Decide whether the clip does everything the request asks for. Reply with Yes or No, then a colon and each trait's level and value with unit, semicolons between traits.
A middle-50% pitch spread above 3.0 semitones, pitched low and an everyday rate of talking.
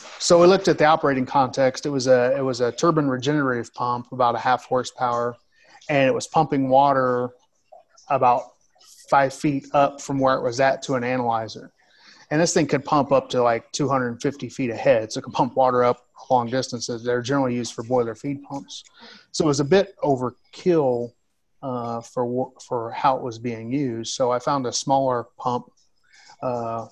No: narrow, 2.5 semitones; low, 130 Hz; average, 185 wpm